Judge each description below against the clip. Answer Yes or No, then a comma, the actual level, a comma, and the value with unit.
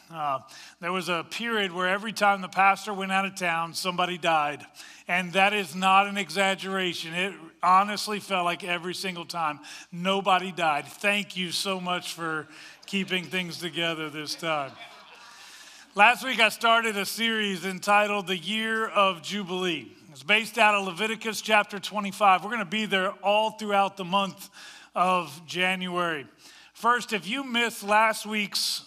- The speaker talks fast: No, average, 160 wpm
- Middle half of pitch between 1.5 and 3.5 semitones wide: Yes, average, 2.8 semitones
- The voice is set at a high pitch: Yes, high, 195 Hz